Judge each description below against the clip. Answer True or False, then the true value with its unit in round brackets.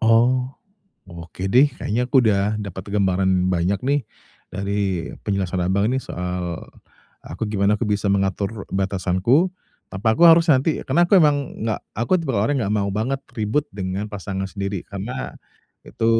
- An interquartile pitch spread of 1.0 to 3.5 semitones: False (4.6 semitones)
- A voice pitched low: True (105 Hz)